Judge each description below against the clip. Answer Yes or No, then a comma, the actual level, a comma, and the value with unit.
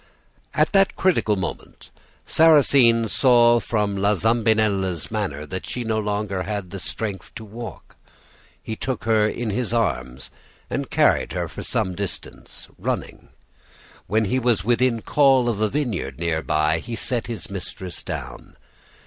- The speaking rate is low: No, average, 145 wpm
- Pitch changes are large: No, average, 3.7 semitones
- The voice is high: No, low, 110 Hz